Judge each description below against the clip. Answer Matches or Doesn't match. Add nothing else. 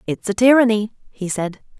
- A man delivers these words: Doesn't match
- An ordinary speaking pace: Matches